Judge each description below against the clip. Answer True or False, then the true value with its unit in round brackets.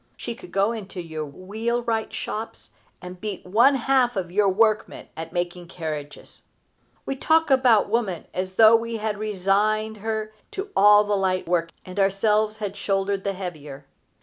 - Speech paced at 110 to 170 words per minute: True (160 wpm)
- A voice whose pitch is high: True (205 Hz)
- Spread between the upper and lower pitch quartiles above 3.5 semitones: False (3.2 semitones)